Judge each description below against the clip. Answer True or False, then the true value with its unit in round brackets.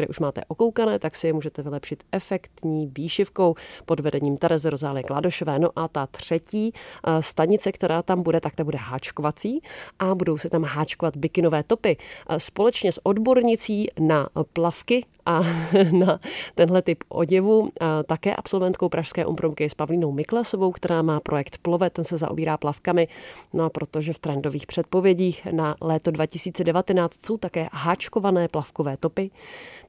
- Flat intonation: False (3.2 semitones)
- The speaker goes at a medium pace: True (150 wpm)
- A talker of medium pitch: True (165 Hz)